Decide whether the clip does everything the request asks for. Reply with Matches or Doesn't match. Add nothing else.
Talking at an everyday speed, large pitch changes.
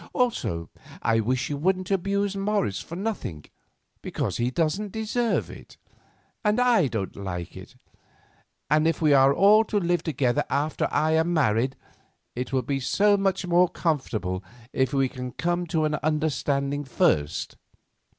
Matches